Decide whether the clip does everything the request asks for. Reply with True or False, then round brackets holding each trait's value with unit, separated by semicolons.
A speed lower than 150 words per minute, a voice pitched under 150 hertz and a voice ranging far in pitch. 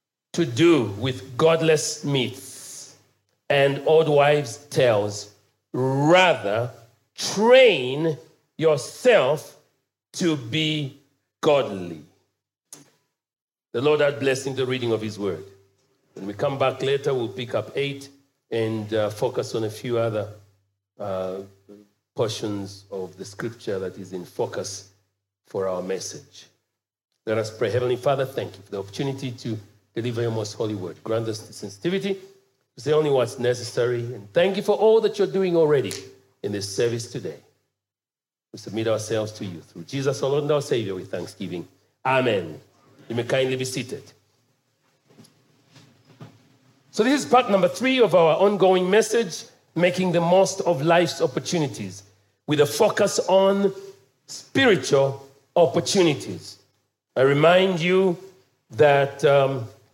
True (140 wpm; 135 Hz; 5.9 semitones)